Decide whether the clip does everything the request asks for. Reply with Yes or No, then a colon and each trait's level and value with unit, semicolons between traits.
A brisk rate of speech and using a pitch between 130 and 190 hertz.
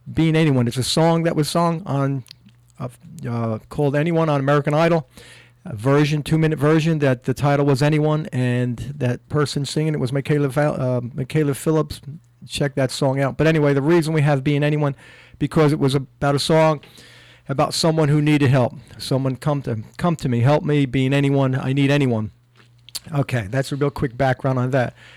No: average, 190 wpm; medium, 140 Hz